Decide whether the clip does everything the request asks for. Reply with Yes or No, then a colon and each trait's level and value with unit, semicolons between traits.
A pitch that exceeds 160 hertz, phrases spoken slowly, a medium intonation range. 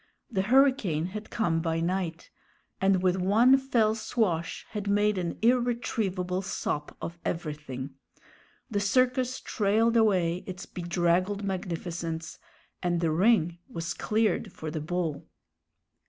Yes: medium, 185 Hz; slow, 125 wpm; average, 4.4 semitones